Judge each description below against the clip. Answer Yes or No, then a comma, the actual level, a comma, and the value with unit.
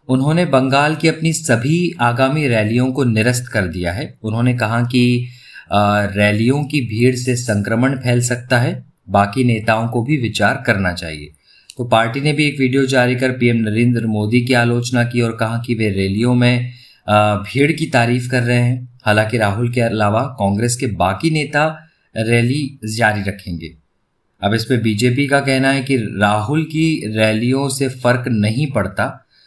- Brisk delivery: No, average, 165 wpm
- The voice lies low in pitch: Yes, low, 120 Hz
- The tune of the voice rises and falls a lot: No, average, 3.4 semitones